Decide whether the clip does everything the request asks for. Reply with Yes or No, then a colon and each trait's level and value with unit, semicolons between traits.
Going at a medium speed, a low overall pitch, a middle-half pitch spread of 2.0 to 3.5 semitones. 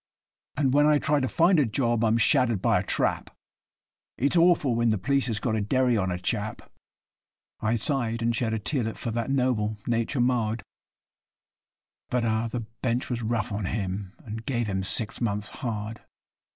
Yes: average, 180 wpm; low, 115 Hz; average, 2.9 semitones